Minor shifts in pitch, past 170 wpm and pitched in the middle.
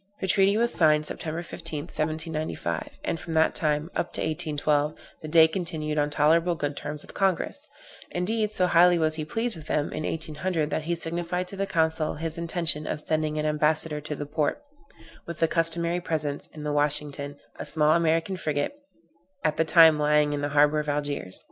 Yes: narrow, 2.0 semitones; average, 190 wpm; medium, 155 Hz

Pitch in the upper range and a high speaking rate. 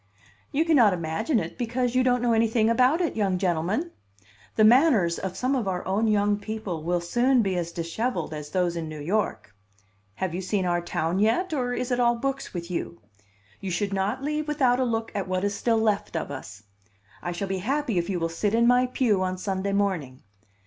Yes: high, 205 Hz; fast, 210 wpm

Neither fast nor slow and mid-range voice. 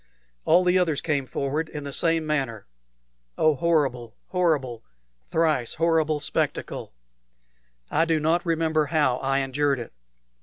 No: slow, 130 wpm; medium, 150 Hz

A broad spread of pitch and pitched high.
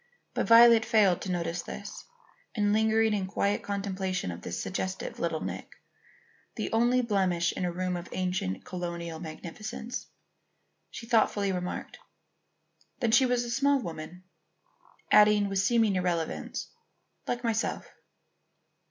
No: average, 3.9 semitones; high, 195 Hz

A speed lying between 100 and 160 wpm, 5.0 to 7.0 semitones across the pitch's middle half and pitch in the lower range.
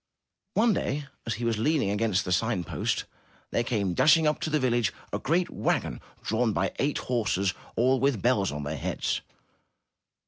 No: average, 180 wpm; wide, 5.6 semitones; low, 115 Hz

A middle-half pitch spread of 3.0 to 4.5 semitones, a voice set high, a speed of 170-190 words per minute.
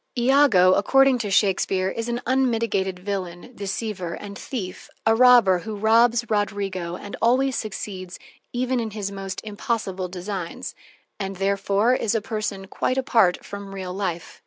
No: average, 3.5 semitones; high, 205 Hz; average, 145 wpm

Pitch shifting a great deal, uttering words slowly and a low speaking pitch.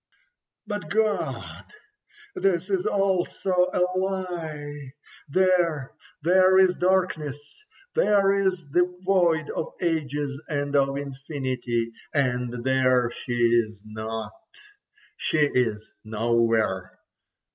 No: wide, 6.9 semitones; slow, 90 wpm; medium, 145 Hz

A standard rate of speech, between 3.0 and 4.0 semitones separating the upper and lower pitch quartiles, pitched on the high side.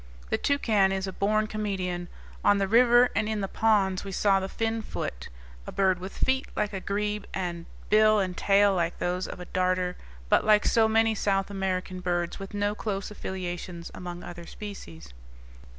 No: average, 180 wpm; narrow, 2.6 semitones; high, 195 Hz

